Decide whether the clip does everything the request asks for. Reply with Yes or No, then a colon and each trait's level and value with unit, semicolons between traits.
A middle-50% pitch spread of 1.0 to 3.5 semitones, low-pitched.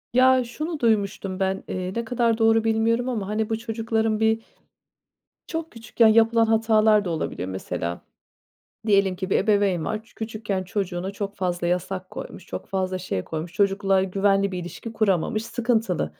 No: average, 3.2 semitones; high, 210 Hz